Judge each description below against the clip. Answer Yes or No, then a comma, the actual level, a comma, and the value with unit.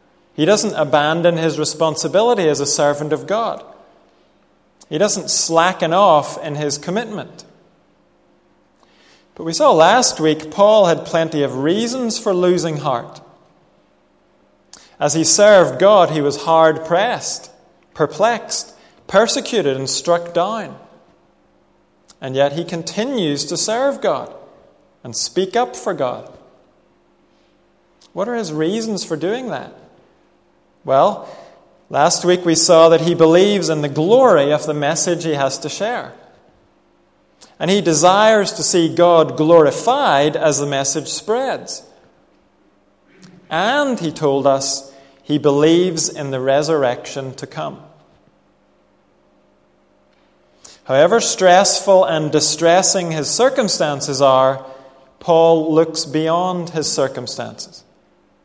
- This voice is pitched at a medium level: Yes, medium, 160 Hz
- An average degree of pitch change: Yes, average, 4.0 semitones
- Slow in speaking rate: Yes, slow, 115 wpm